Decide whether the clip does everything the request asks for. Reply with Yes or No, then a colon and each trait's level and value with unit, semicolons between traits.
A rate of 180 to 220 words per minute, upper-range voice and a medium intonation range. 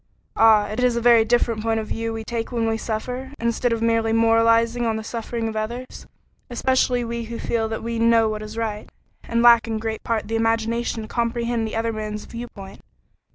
No: fast, 205 wpm; high, 230 Hz; narrow, 1.0 semitones